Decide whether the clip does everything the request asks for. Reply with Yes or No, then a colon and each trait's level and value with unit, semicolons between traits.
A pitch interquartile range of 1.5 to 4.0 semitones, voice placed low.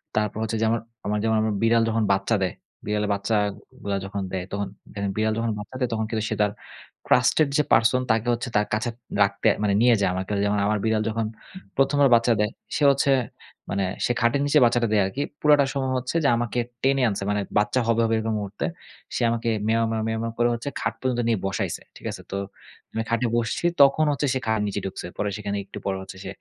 Yes: average, 2.7 semitones; low, 110 Hz